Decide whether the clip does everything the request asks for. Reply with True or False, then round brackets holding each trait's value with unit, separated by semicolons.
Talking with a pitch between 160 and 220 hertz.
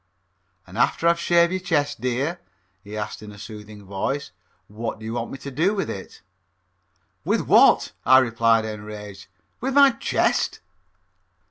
False (120 Hz)